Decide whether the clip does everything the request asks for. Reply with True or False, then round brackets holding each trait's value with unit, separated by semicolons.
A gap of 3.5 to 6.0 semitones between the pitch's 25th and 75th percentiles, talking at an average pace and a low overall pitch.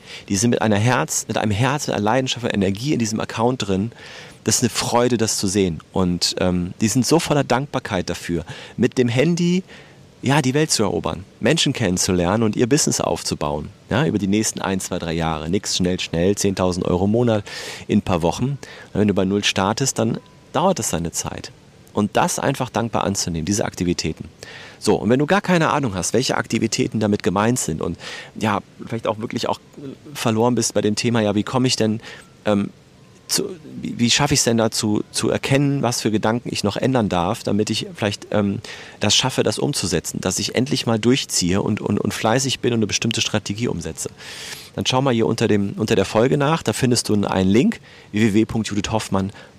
False (4.0 semitones; 205 wpm; 110 Hz)